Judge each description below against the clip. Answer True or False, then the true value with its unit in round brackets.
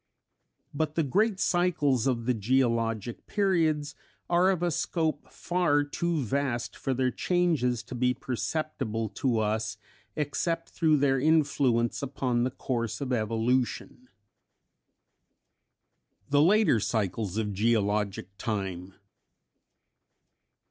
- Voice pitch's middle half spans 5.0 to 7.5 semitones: True (5.5 semitones)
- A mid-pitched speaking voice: False (130 Hz)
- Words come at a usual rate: False (110 wpm)